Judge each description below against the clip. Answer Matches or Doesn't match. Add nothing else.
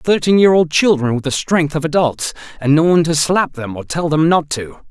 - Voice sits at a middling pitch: Matches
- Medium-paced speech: Doesn't match